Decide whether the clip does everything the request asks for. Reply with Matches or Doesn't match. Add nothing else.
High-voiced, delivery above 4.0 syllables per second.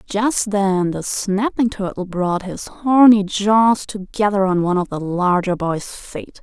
Doesn't match